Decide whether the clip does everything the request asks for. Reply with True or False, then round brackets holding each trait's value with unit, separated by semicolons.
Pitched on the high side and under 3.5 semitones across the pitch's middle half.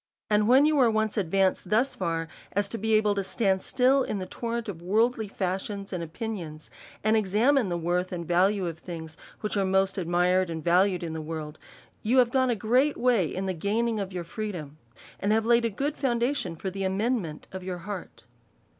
False (195 Hz; 4.2 semitones)